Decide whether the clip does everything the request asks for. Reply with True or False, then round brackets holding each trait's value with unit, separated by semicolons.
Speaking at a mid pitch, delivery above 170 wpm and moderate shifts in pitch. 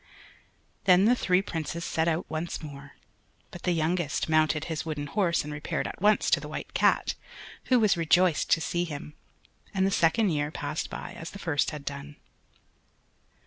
True (165 Hz; 180 wpm; 3.1 semitones)